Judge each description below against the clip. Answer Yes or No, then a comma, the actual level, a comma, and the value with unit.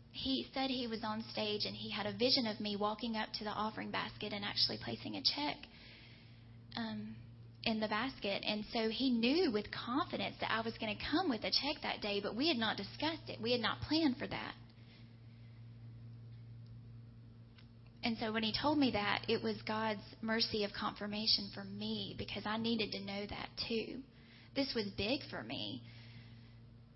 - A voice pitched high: Yes, high, 205 Hz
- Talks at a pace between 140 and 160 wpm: No, average, 185 wpm